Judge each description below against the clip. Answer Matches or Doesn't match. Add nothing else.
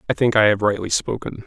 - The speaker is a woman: Doesn't match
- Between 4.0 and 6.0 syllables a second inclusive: Doesn't match